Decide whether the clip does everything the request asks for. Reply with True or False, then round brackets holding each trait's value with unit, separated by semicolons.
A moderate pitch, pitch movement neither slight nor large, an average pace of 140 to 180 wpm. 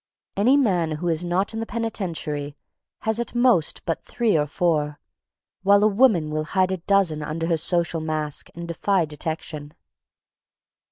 True (170 Hz; 4.6 semitones; 160 wpm)